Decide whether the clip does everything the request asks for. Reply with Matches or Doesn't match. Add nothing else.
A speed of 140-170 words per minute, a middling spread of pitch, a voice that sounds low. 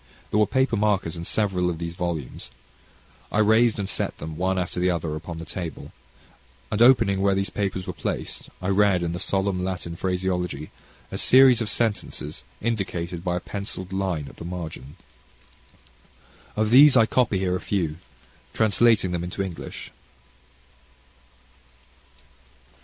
Matches